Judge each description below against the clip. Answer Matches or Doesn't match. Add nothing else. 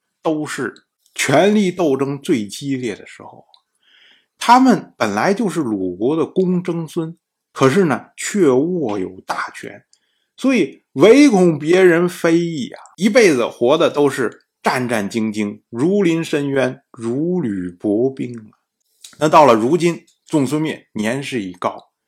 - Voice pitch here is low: Doesn't match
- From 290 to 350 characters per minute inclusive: Doesn't match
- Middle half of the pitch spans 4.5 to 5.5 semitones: Matches